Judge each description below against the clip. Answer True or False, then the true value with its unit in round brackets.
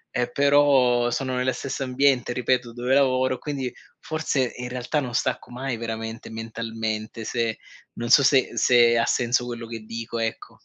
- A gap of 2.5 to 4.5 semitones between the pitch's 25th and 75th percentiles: False (2.1 semitones)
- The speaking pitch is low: True (125 Hz)